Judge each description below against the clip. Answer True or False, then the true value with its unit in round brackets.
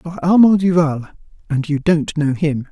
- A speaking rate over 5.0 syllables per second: False (4.0 syllables/s)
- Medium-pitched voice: True (160 Hz)